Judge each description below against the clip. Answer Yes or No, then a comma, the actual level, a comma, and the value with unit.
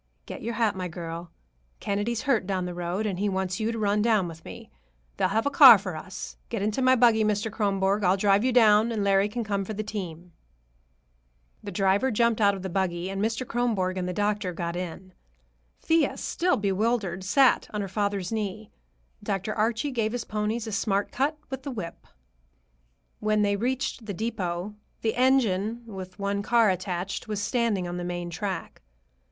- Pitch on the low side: No, high, 205 Hz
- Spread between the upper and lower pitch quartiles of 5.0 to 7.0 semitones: No, average, 3.2 semitones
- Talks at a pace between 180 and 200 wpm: Yes, average, 190 wpm